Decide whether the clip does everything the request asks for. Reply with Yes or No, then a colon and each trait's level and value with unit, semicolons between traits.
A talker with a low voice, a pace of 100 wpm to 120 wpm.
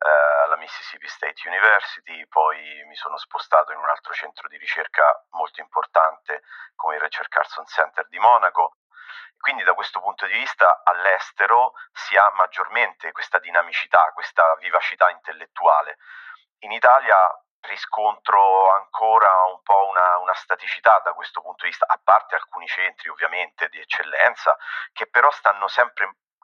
No: low, 110 Hz; average, 145 wpm